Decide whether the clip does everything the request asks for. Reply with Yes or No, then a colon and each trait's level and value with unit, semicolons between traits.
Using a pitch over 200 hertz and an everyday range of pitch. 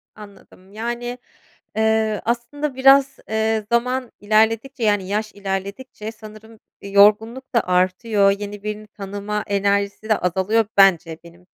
No: high, 215 Hz; narrow, 2.3 semitones